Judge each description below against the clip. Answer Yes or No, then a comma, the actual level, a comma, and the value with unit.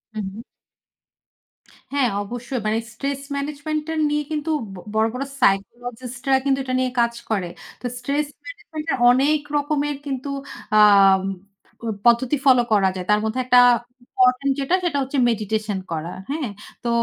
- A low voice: No, very high, 255 Hz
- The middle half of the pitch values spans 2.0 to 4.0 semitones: No, average, 4.4 semitones